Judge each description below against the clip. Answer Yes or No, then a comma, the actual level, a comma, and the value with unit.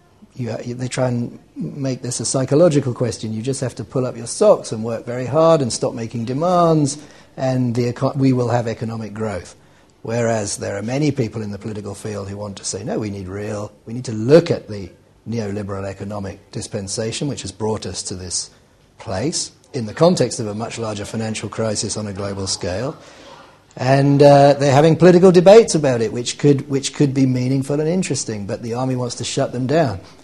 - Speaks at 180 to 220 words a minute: Yes, average, 200 wpm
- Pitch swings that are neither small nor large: Yes, average, 4.2 semitones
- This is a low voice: Yes, low, 120 Hz